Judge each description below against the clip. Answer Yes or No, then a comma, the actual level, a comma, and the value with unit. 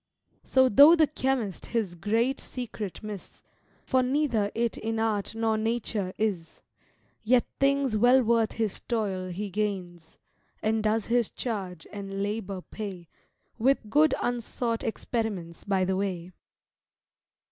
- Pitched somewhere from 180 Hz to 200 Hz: No, high, 220 Hz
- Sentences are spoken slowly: Yes, slow, 130 wpm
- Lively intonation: No, average, 3.5 semitones